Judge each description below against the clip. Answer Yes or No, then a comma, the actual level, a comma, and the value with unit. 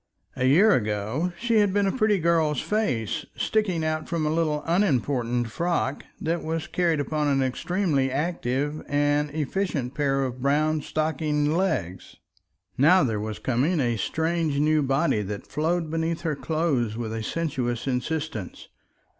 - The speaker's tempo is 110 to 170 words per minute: Yes, average, 150 wpm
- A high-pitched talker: No, medium, 150 Hz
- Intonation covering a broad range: No, average, 4.3 semitones